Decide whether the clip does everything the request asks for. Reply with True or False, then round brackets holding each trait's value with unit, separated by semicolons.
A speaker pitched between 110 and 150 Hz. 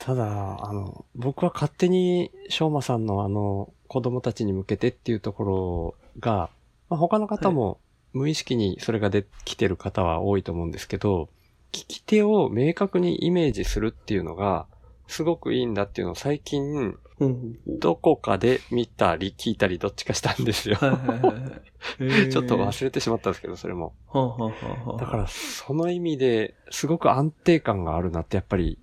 True (115 Hz)